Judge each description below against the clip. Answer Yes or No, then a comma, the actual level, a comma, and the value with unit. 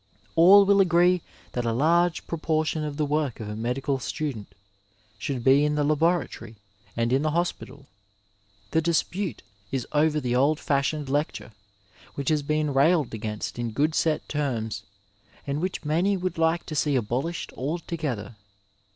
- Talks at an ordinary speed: Yes, average, 160 wpm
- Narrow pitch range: No, average, 3.8 semitones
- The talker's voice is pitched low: No, medium, 150 Hz